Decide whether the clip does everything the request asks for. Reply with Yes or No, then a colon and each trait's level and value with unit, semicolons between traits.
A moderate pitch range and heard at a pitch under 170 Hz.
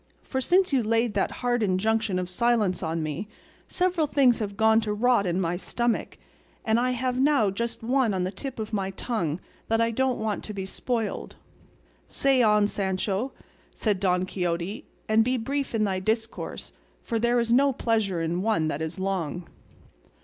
No: average, 4.2 semitones; high, 220 Hz